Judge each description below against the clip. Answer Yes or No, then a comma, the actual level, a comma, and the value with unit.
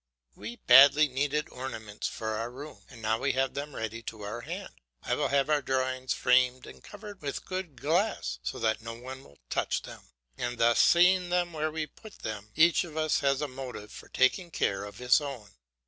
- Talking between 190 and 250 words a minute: Yes, fast, 205 wpm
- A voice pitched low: Yes, low, 130 Hz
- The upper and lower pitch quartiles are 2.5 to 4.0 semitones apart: No, average, 4.9 semitones